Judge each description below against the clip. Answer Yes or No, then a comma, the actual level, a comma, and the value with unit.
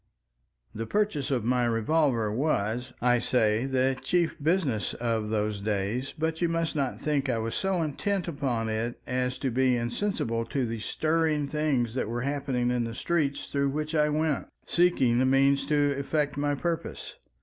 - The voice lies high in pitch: No, low, 135 Hz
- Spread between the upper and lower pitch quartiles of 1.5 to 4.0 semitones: No, average, 4.5 semitones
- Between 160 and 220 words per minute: Yes, average, 170 wpm